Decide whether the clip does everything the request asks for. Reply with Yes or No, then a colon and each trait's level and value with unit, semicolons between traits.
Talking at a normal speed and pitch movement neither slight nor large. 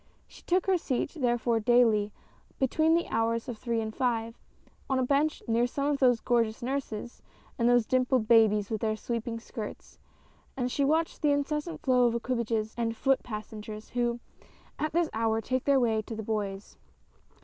Yes: average, 180 wpm; average, 3.2 semitones